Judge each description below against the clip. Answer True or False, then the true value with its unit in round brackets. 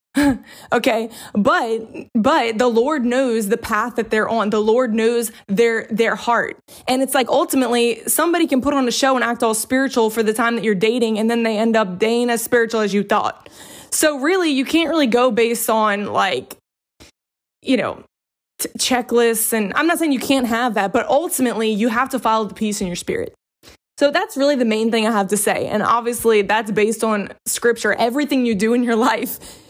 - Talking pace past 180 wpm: True (205 wpm)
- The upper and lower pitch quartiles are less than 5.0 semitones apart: True (3.0 semitones)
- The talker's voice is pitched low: False (235 Hz)